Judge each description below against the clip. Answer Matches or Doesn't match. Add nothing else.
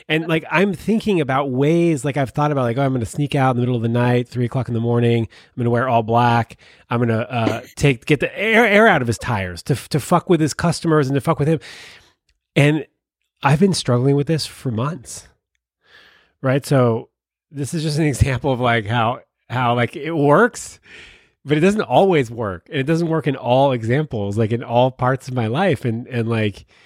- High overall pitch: Doesn't match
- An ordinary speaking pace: Doesn't match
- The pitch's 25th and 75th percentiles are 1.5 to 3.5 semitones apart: Doesn't match